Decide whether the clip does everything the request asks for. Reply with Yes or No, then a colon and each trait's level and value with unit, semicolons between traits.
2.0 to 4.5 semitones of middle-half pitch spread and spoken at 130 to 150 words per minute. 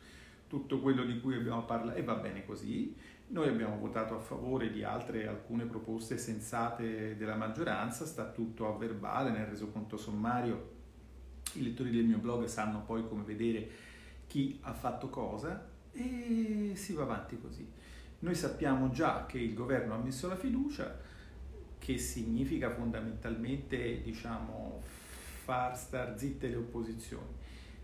Yes: average, 2.9 semitones; average, 140 wpm